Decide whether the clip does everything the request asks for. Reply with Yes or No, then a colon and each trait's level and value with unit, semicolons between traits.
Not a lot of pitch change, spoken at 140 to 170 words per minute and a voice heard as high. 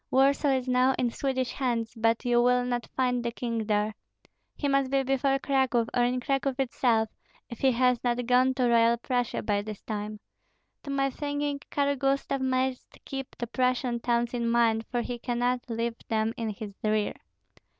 No: narrow, 2.2 semitones; average, 180 wpm; high, 245 Hz